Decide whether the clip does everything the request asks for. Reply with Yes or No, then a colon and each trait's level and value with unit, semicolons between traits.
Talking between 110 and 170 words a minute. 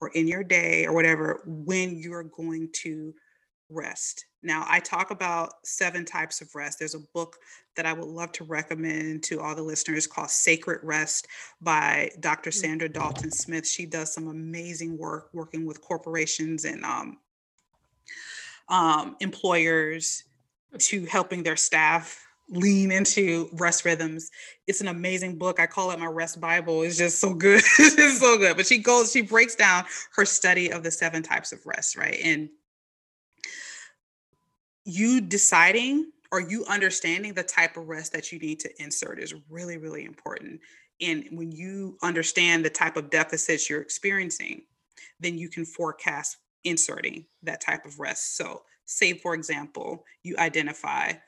Yes: average, 160 wpm